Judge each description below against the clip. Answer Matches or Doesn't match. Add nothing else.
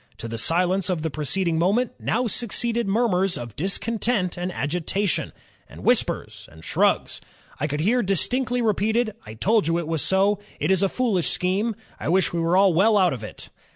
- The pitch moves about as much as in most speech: Matches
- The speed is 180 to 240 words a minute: Matches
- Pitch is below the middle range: Doesn't match